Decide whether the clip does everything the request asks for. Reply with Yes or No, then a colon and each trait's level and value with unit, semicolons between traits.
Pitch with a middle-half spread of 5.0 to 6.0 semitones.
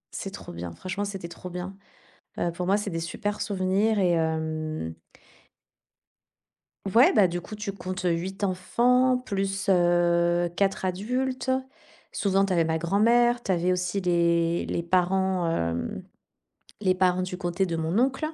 No: average, 2.7 semitones